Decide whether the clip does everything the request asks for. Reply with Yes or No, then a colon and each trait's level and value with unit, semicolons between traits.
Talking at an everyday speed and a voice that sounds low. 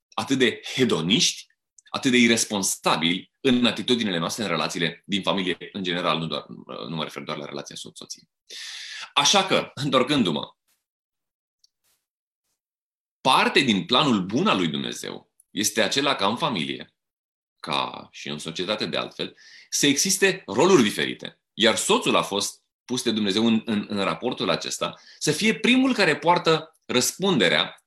Yes: average, 145 wpm; low, 110 Hz